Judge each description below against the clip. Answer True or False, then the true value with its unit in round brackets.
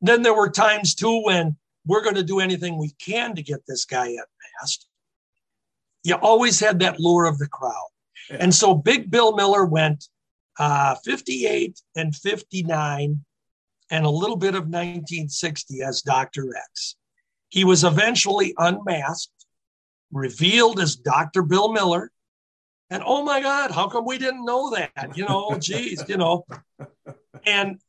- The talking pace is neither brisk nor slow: True (150 wpm)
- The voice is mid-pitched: True (175 Hz)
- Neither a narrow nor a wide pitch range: False (6.1 semitones)